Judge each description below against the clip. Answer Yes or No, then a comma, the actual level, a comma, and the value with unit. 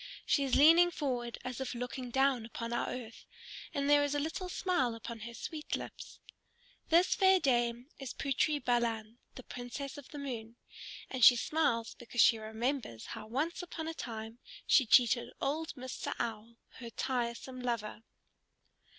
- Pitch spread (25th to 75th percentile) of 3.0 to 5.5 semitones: Yes, average, 3.6 semitones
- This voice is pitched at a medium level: No, very high, 250 Hz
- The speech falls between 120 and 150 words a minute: No, average, 160 wpm